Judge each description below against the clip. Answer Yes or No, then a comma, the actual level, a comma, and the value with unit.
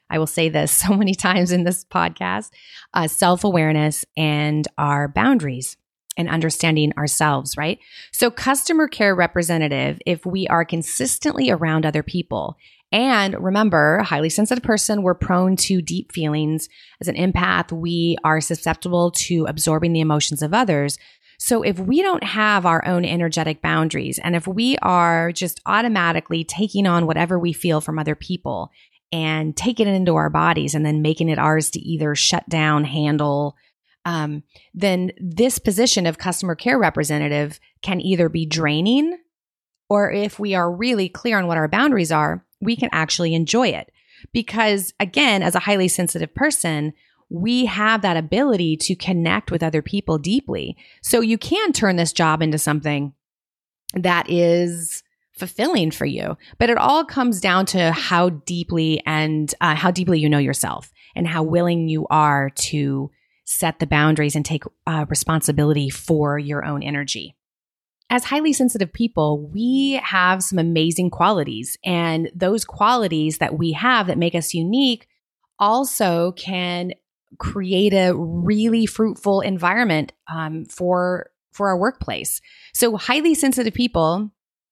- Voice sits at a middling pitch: Yes, medium, 175 Hz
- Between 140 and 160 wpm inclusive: Yes, average, 155 wpm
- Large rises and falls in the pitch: No, average, 4.7 semitones